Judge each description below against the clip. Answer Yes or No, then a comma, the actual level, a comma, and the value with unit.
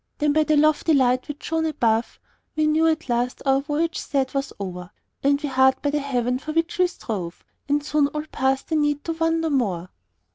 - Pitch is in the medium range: No, very high, 290 Hz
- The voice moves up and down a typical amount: Yes, average, 3.2 semitones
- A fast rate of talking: Yes, fast, 210 wpm